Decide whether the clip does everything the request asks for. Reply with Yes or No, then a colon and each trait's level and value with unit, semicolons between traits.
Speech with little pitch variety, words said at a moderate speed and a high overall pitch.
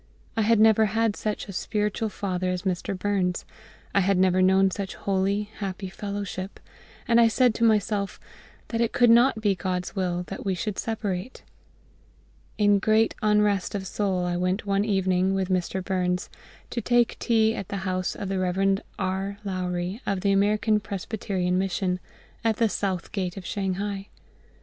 Yes: narrow, 2.3 semitones; average, 170 wpm; high, 195 Hz